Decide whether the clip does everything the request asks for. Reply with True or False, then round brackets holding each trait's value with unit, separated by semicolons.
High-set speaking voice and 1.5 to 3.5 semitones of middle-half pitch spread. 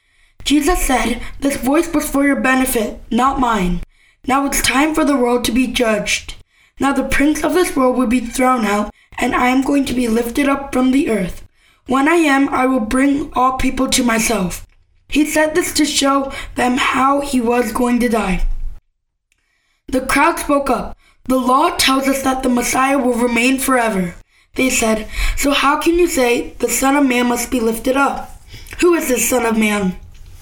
True (260 Hz; 2.5 semitones)